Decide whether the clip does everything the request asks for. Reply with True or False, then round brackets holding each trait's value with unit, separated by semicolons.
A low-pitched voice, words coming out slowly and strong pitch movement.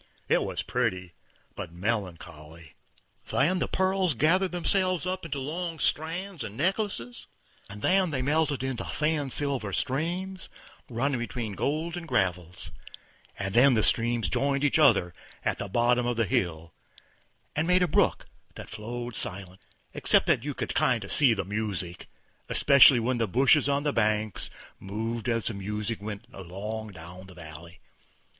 False (120 Hz; 150 wpm; 7.1 semitones)